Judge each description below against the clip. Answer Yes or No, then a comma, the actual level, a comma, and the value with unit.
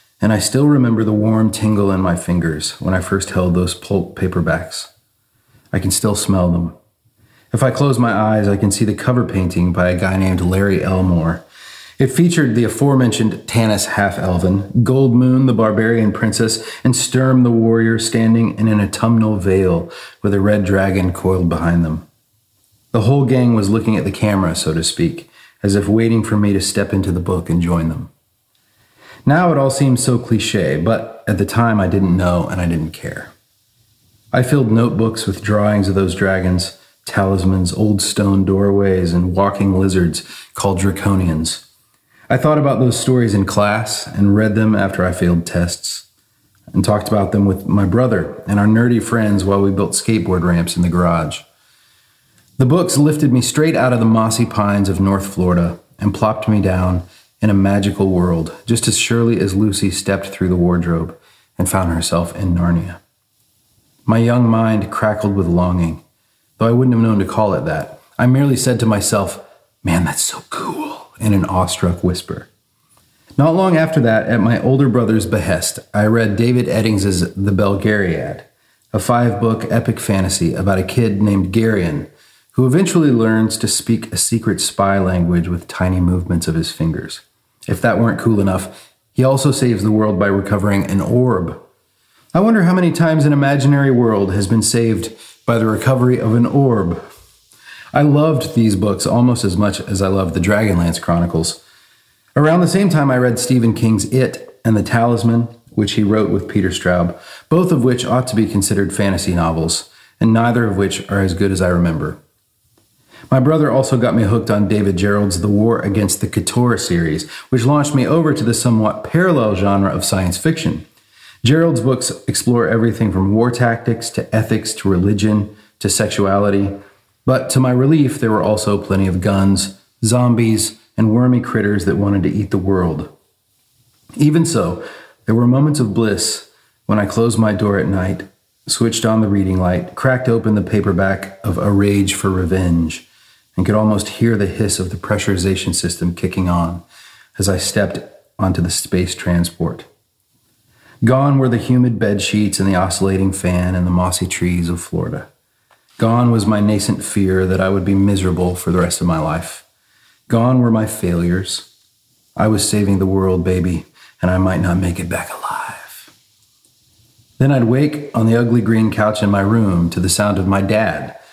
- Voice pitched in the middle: No, low, 105 Hz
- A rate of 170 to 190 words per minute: Yes, average, 180 wpm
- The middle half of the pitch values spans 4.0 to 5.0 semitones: No, average, 3.5 semitones